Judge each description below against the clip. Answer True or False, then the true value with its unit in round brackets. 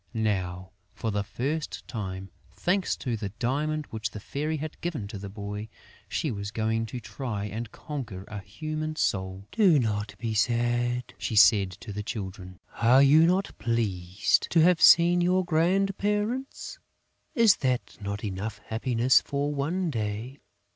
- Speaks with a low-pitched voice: True (115 Hz)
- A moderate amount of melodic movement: False (6.9 semitones)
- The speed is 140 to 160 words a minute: True (155 wpm)